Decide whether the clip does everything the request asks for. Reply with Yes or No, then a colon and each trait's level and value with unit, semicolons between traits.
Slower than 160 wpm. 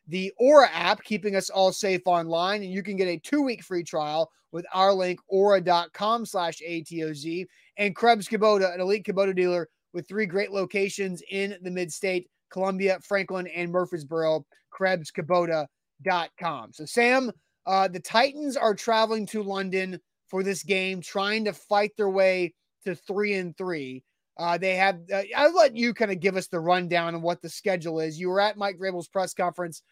No: average, 180 wpm